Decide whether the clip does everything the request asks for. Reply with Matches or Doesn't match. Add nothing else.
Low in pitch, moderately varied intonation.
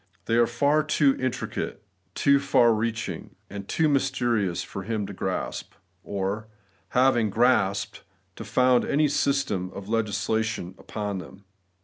Matches